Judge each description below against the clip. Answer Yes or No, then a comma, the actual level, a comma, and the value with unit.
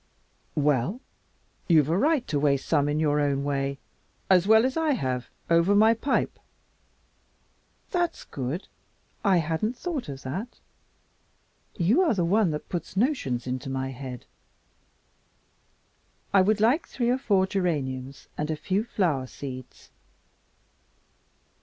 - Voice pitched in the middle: Yes, medium, 170 Hz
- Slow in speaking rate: Yes, slow, 130 wpm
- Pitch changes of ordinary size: No, wide, 7.9 semitones